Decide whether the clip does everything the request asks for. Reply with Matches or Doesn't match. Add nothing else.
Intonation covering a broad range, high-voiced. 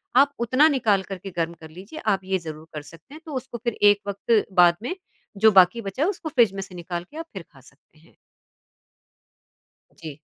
Matches